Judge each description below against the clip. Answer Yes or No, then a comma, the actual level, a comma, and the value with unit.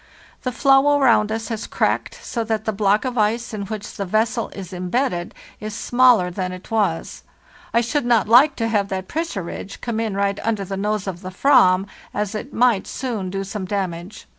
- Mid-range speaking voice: No, high, 215 Hz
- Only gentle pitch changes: No, average, 3.4 semitones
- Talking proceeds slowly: No, average, 200 wpm